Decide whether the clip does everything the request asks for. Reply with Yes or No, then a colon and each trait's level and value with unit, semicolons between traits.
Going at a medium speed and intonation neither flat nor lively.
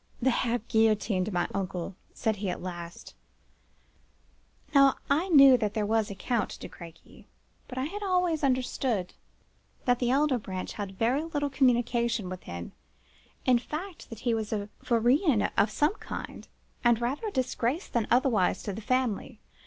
Yes: average, 160 wpm; average, 4.5 semitones